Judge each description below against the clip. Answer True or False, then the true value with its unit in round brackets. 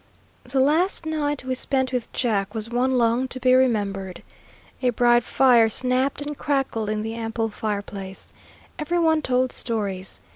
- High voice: True (250 Hz)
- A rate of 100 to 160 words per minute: True (155 wpm)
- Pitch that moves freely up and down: False (3.2 semitones)